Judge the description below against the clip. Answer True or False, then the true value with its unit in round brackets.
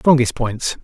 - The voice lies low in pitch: True (125 Hz)